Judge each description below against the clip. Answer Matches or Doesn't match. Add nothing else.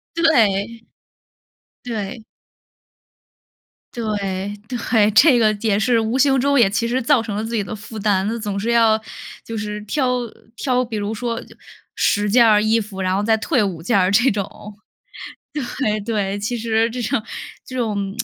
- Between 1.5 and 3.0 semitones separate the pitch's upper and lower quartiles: Matches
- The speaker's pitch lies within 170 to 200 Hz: Doesn't match